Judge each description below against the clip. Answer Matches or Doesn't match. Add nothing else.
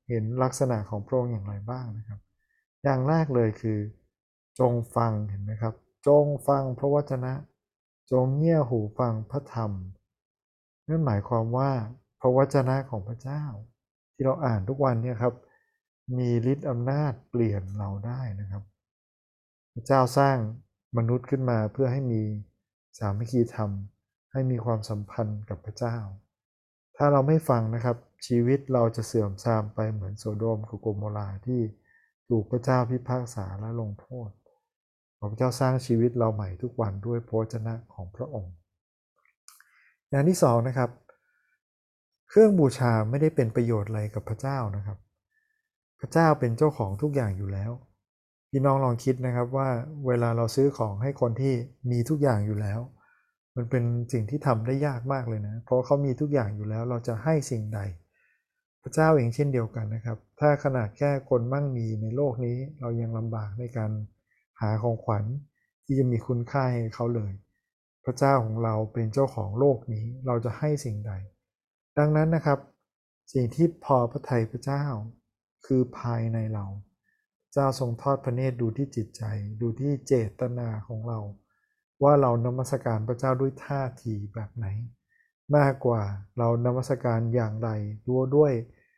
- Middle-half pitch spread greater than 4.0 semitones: Doesn't match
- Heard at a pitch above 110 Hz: Matches